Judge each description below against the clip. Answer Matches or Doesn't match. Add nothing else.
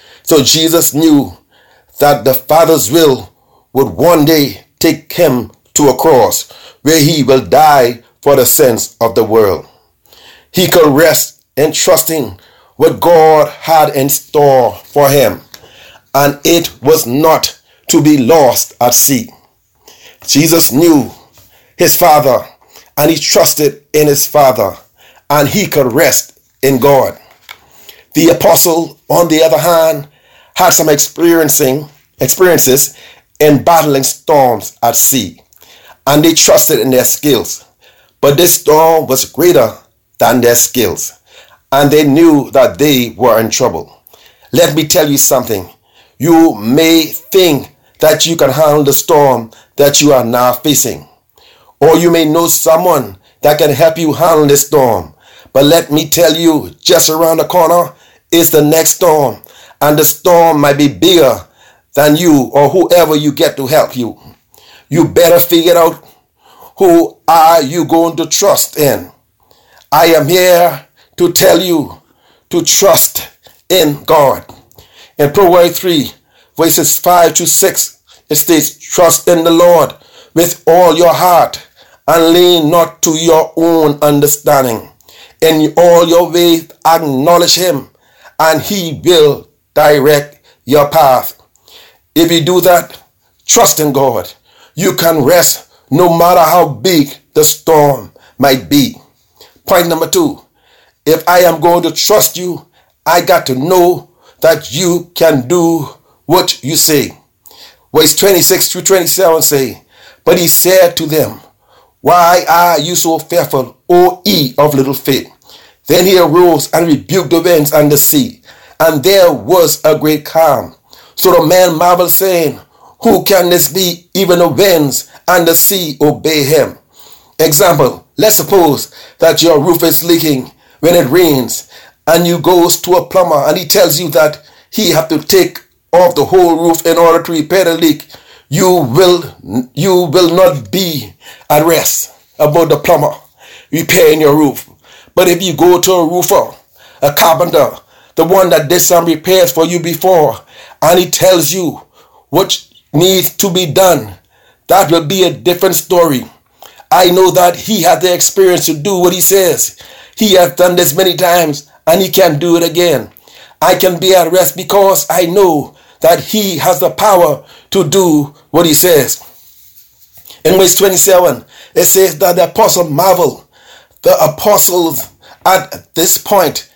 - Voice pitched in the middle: Matches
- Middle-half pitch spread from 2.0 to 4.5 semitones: Matches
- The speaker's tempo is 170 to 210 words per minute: Doesn't match